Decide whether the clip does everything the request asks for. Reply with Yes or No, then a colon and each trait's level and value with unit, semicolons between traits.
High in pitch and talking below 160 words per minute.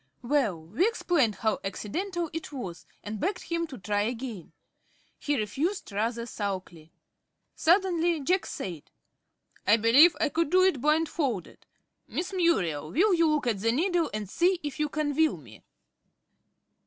Yes: very high, 285 Hz; average, 150 wpm